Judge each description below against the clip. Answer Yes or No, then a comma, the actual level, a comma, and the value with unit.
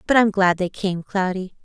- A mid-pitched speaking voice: No, high, 195 Hz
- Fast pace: Yes, fast, 220 wpm